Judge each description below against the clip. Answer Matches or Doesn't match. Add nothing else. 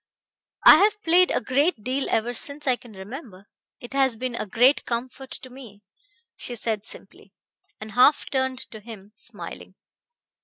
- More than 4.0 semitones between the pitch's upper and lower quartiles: Doesn't match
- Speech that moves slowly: Doesn't match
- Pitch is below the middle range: Doesn't match